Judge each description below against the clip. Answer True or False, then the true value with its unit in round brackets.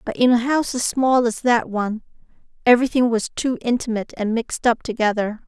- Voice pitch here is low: False (235 Hz)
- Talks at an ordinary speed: True (185 wpm)